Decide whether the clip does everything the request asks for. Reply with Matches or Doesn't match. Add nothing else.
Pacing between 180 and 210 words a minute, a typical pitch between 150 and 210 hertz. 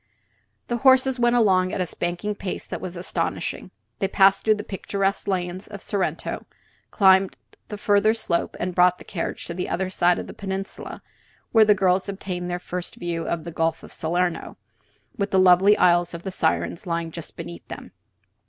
Matches